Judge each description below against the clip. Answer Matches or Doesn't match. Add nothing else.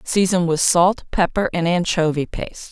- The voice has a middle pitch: Matches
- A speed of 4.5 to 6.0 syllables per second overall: Matches